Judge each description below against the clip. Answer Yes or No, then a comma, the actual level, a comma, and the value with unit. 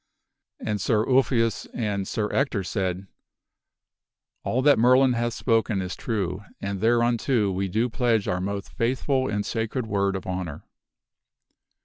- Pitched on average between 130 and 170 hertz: No, low, 110 Hz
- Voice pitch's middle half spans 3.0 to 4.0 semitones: Yes, average, 3.6 semitones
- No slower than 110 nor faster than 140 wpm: Yes, slow, 135 wpm